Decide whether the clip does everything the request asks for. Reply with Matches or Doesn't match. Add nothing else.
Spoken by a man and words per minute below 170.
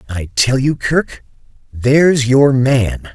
Matches